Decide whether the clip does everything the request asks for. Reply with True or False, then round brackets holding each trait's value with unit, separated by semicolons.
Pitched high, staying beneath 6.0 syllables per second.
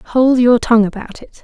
True (235 Hz; 5.0 syllables/s)